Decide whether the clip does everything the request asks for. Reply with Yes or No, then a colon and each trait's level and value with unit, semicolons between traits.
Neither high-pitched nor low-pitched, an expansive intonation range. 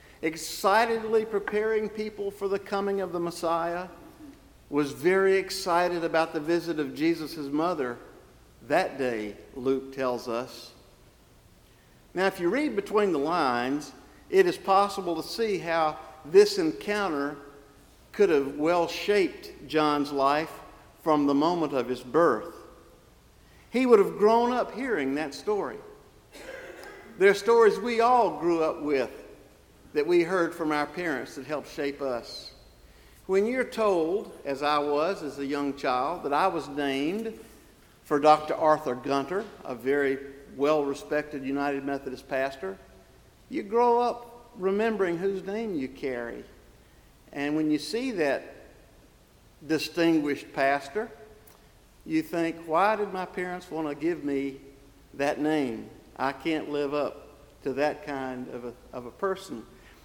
Yes: medium, 160 Hz; wide, 6.0 semitones